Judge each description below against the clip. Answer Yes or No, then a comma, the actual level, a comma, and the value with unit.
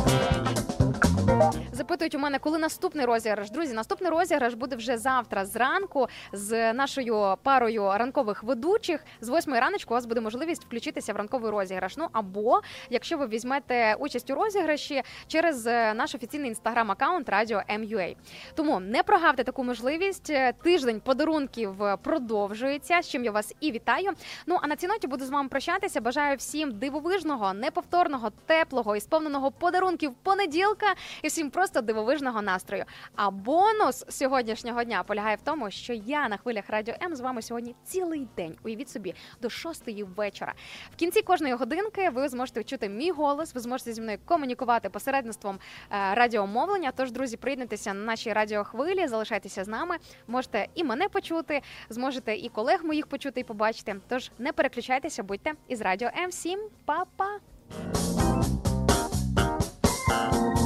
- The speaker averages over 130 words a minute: Yes, average, 145 wpm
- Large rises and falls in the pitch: Yes, wide, 6.2 semitones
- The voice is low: No, very high, 260 Hz